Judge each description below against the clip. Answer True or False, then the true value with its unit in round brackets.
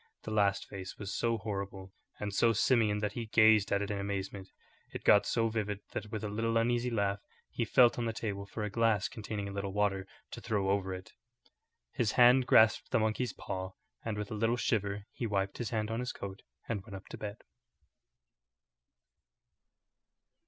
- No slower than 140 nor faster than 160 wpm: False (190 wpm)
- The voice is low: True (105 Hz)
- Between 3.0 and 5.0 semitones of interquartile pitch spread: False (2.4 semitones)